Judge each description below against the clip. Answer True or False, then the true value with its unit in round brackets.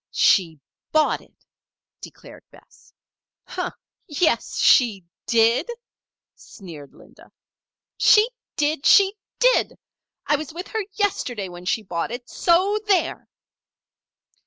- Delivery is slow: True (105 wpm)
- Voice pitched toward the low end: False (280 Hz)